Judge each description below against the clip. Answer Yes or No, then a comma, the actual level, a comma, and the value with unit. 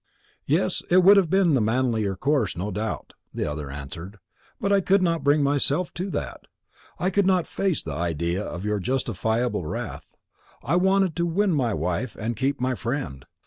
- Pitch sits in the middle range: No, low, 130 Hz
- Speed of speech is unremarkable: Yes, average, 185 wpm